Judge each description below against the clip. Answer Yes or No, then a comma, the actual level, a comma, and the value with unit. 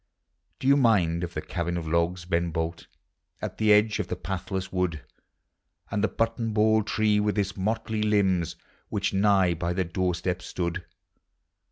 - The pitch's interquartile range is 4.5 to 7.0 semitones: No, average, 3.5 semitones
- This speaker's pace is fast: No, average, 165 wpm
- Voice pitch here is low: Yes, very low, 95 Hz